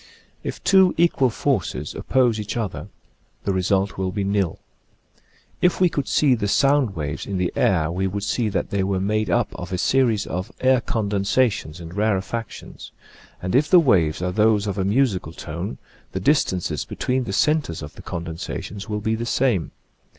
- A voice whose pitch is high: No, low, 100 Hz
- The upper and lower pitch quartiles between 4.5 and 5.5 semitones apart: Yes, average, 5.0 semitones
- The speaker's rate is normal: Yes, average, 180 wpm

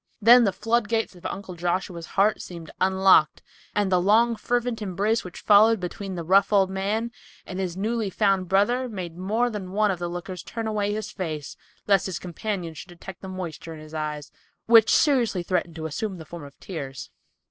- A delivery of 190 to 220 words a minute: Yes, average, 195 wpm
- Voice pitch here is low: No, high, 190 Hz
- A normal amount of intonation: Yes, average, 3.6 semitones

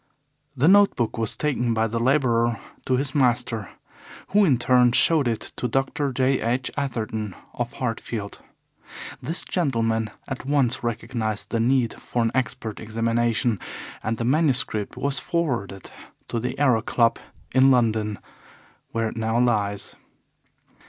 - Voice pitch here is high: No, low, 120 Hz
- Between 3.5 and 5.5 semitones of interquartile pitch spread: No, average, 2.8 semitones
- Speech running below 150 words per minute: Yes, average, 140 wpm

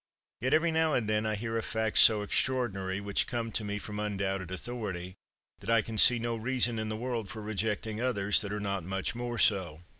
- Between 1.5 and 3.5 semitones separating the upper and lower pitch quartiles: Yes, average, 2.8 semitones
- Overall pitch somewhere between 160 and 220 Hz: No, low, 110 Hz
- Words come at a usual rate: No, fast, 215 wpm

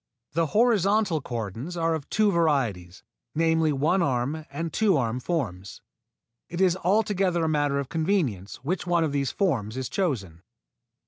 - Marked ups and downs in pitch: Yes, wide, 5.7 semitones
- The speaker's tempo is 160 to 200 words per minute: No, average, 150 wpm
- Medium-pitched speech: Yes, medium, 160 Hz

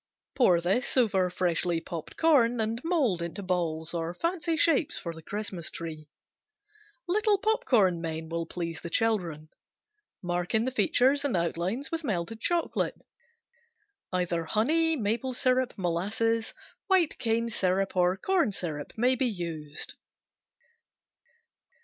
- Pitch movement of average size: No, wide, 7.1 semitones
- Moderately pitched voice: No, high, 200 Hz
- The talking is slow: Yes, slow, 125 wpm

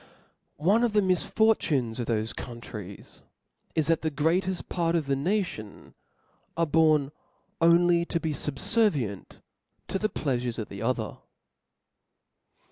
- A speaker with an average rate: No, slow, 125 wpm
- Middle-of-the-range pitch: Yes, medium, 155 Hz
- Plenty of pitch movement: Yes, wide, 6.4 semitones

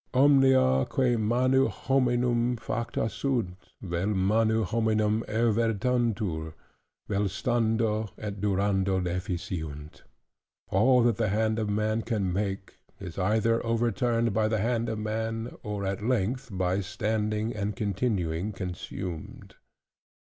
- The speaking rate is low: Yes, slow, 115 wpm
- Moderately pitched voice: No, low, 110 Hz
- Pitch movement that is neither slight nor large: Yes, average, 3.2 semitones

